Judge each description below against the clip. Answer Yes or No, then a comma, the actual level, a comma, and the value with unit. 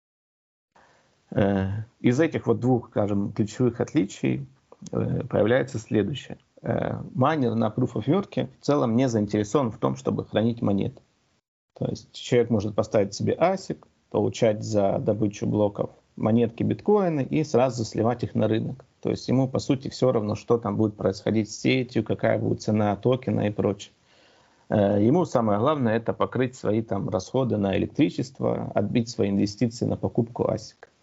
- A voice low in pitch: Yes, low, 110 Hz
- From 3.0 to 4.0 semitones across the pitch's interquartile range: Yes, average, 3.3 semitones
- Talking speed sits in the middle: Yes, average, 145 wpm